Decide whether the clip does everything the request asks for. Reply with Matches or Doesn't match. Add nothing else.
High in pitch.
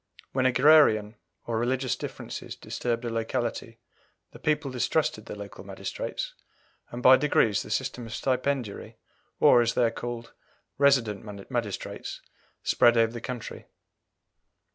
Doesn't match